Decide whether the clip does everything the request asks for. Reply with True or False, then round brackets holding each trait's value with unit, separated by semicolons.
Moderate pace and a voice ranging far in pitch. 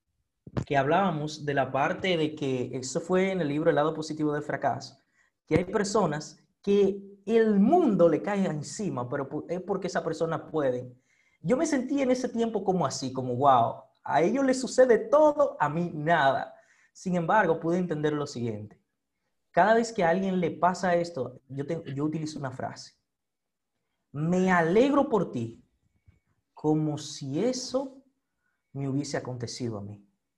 True (160 wpm; 6.3 semitones)